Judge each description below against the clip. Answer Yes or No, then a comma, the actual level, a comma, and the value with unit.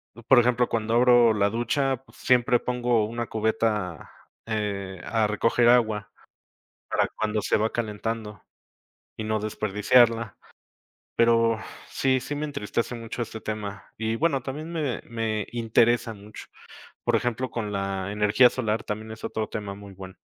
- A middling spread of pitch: No, narrow, 2.3 semitones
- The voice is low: Yes, low, 115 Hz